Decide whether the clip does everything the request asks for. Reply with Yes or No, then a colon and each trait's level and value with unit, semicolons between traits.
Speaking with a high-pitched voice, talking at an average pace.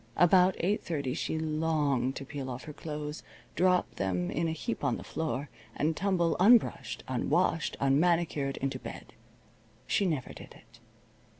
No: medium, 155 Hz; average, 155 wpm